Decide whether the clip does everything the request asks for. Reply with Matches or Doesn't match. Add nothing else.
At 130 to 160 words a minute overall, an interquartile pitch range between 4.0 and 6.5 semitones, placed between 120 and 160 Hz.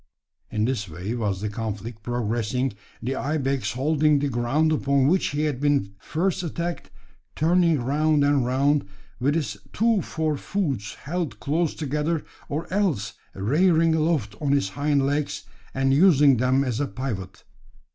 Matches